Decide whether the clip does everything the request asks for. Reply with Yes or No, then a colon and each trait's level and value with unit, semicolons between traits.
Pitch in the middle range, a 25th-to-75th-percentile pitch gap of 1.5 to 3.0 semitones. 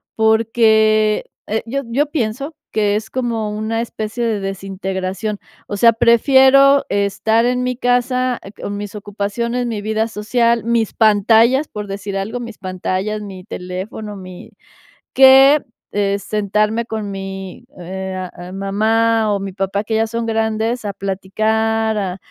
No: high, 215 Hz; narrow, 2.6 semitones